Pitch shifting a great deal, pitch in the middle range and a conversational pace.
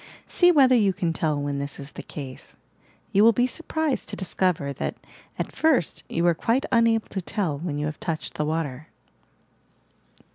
Yes: wide, 7.5 semitones; medium, 175 Hz; average, 180 wpm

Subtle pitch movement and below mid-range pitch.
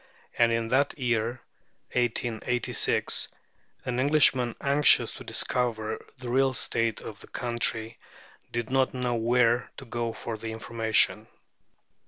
Yes: narrow, 1.6 semitones; low, 120 Hz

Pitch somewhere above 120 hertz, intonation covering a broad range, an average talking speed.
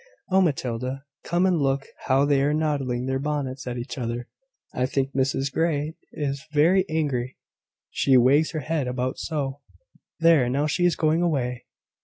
No: medium, 140 Hz; average, 3.2 semitones; average, 165 wpm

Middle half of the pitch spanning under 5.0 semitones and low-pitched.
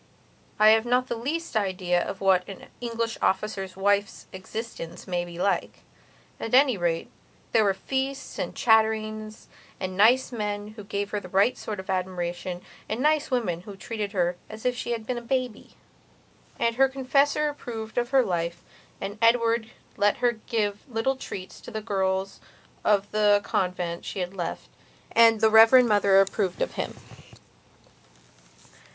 No: average, 3.7 semitones; high, 215 Hz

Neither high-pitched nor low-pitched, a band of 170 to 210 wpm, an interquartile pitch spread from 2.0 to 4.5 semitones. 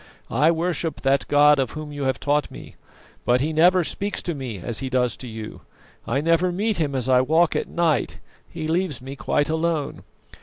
Yes: medium, 150 Hz; average, 200 wpm; average, 4.0 semitones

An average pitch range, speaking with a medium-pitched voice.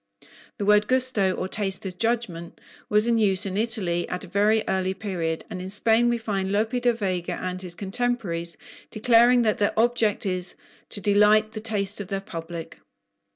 No: average, 3.3 semitones; high, 205 Hz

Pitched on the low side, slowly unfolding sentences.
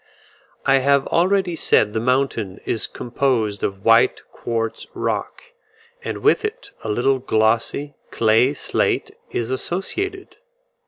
Yes: low, 130 Hz; slow, 120 wpm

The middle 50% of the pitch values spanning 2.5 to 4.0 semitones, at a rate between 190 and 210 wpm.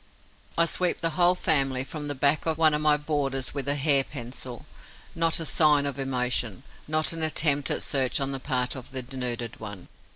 Yes: average, 3.2 semitones; average, 200 wpm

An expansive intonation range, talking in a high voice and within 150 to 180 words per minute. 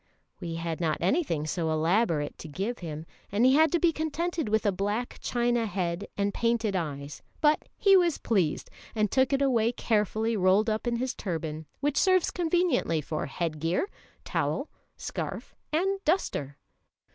Yes: wide, 8.6 semitones; high, 215 Hz; average, 165 wpm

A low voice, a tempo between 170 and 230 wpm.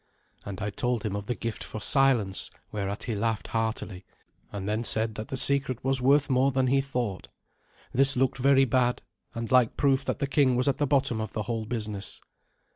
Yes: low, 120 Hz; average, 200 wpm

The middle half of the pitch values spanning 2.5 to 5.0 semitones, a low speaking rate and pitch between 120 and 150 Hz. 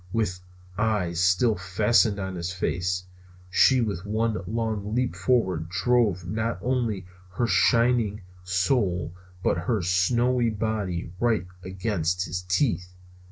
No: average, 4.2 semitones; slow, 120 wpm; low, 100 Hz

